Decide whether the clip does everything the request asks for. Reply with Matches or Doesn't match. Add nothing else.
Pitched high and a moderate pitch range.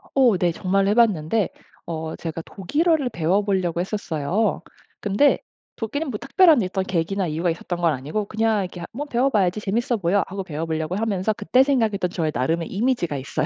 Matches